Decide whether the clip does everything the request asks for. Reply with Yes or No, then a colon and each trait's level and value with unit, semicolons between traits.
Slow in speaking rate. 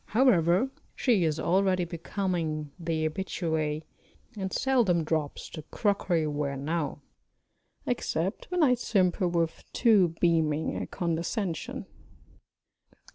Yes: slow, 105 wpm